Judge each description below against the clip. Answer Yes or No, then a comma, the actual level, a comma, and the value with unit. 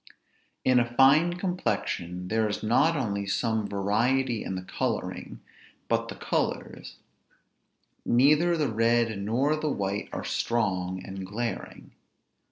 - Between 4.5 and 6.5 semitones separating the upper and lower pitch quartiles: Yes, average, 5.0 semitones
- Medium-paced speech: No, slow, 125 wpm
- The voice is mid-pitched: No, low, 115 Hz